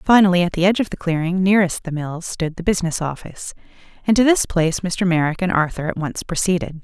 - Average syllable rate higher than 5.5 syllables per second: Yes, 6.5 syllables/s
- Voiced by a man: No, female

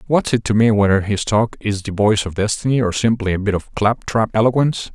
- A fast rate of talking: Yes, fast, 245 wpm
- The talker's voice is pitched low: Yes, low, 110 Hz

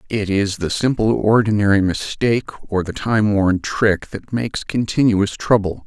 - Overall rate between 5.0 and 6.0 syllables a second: No, 4.4 syllables/s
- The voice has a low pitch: Yes, low, 105 Hz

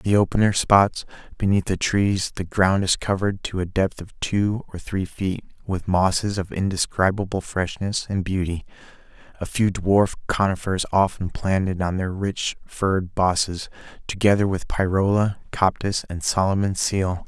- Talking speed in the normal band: Yes, average, 155 wpm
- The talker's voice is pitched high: No, very low, 95 Hz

